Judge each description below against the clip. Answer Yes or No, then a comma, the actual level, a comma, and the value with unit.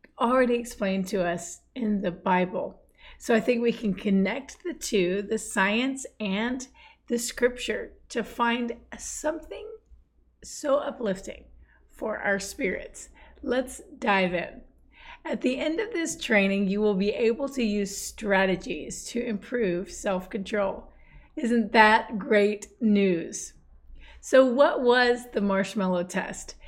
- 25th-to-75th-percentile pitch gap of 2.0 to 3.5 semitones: No, average, 4.2 semitones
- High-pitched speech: Yes, high, 220 Hz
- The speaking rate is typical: No, slow, 130 wpm